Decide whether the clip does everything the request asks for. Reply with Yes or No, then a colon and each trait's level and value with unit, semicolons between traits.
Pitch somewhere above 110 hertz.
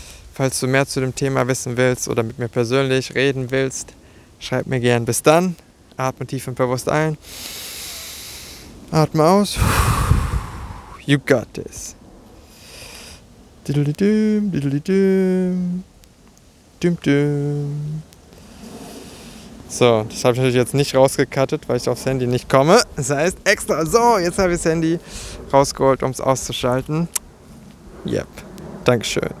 Yes: low, 135 Hz